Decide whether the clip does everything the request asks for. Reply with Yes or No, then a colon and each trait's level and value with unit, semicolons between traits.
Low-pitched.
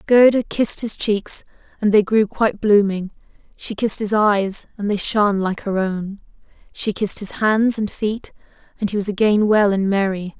No: high, 205 Hz